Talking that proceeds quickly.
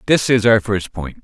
Yes: fast, 245 wpm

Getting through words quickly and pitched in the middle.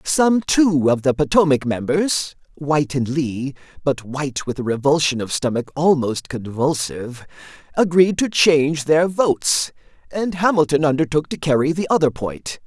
No: average, 145 wpm; medium, 150 Hz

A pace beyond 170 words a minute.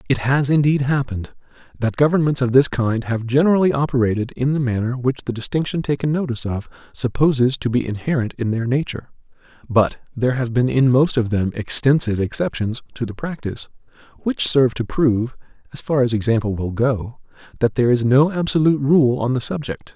Yes: average, 180 wpm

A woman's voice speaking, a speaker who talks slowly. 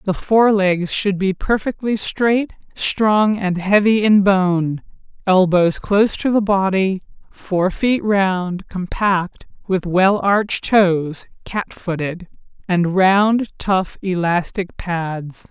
Yes: female; slow, 125 wpm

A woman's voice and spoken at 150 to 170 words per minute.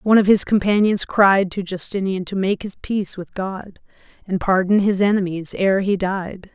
No: female; average, 185 wpm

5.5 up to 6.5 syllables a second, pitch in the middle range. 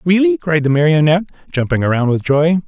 Yes: 6.3 syllables/s; medium, 160 Hz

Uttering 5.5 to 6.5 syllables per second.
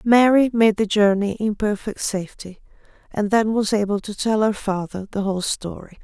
No: 5.1 syllables/s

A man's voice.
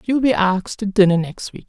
No: female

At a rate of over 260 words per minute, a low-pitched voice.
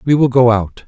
Yes: fast, 275 wpm; low, 125 Hz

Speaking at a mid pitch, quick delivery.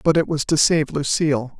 Yes: medium, 150 Hz; fast, 225 wpm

